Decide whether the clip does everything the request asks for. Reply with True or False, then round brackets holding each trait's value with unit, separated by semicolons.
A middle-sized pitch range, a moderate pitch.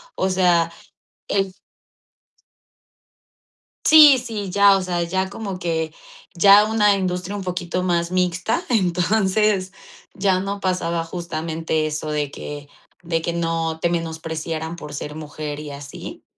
True (3.1 semitones; 175 Hz)